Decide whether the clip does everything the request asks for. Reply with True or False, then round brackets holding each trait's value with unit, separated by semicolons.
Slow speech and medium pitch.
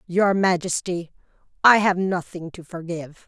True (130 wpm; 180 Hz)